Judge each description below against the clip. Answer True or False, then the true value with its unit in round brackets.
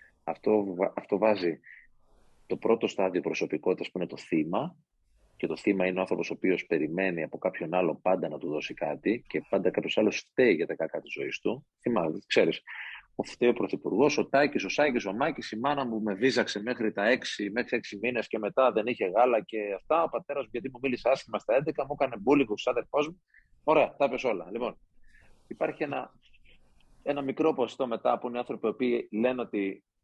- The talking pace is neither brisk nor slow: False (200 wpm)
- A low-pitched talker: True (120 Hz)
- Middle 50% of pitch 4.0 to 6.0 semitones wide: True (4.8 semitones)